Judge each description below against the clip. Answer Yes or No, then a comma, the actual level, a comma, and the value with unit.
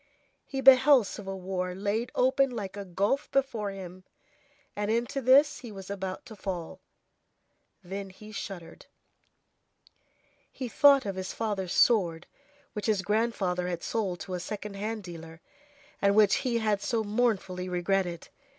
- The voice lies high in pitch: Yes, high, 200 Hz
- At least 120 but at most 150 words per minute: Yes, average, 145 wpm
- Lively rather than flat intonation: No, average, 3.8 semitones